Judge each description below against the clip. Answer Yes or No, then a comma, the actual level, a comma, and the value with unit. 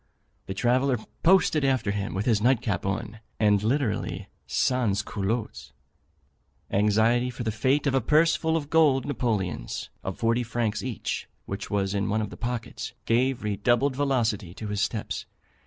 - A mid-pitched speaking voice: No, low, 115 Hz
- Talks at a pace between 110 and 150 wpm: No, average, 160 wpm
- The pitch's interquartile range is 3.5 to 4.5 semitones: Yes, average, 4.1 semitones